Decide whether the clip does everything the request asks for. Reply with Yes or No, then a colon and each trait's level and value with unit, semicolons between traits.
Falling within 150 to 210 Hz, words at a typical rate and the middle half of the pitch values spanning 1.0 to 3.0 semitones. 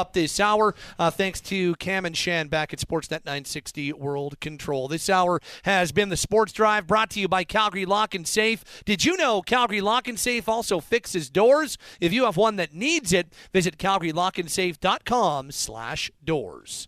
No: high, 190 Hz; average, 180 wpm; average, 4.7 semitones